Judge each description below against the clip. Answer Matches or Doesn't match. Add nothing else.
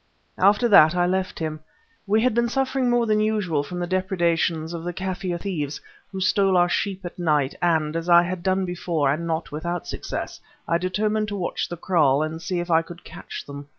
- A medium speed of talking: Doesn't match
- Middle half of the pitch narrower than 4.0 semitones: Matches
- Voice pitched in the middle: Matches